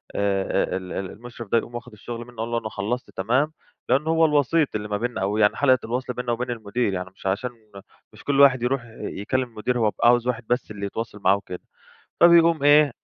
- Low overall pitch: Yes, low, 120 Hz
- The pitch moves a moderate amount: Yes, average, 3.9 semitones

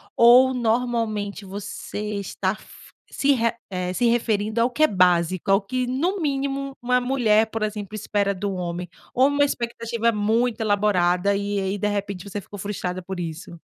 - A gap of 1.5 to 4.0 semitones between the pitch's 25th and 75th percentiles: Yes, average, 3.6 semitones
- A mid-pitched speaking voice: No, high, 210 Hz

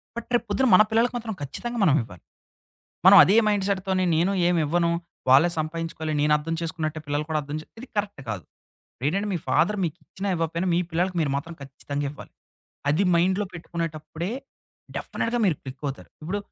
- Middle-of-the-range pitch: Yes, medium, 165 Hz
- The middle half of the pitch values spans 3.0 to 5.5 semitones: Yes, average, 4.2 semitones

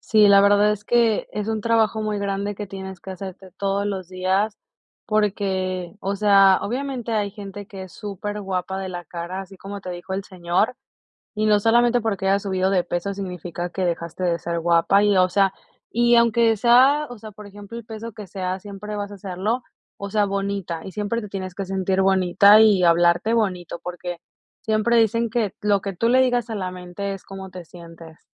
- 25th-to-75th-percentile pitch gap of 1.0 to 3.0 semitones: Yes, narrow, 2.4 semitones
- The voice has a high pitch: Yes, high, 200 Hz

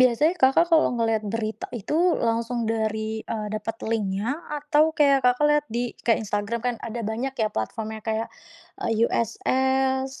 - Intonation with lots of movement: No, average, 3.4 semitones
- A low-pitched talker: No, high, 230 Hz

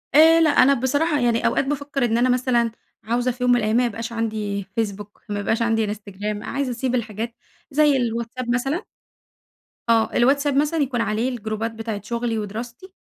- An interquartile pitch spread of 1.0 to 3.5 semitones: Yes, average, 3.0 semitones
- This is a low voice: No, high, 235 Hz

